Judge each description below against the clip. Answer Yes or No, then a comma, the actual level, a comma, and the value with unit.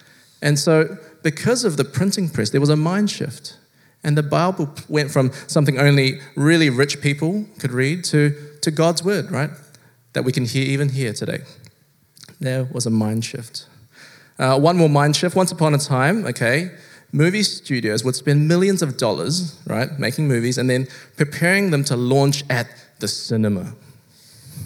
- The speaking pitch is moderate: Yes, medium, 145 Hz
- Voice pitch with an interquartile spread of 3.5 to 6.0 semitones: Yes, average, 3.9 semitones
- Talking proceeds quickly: No, average, 170 wpm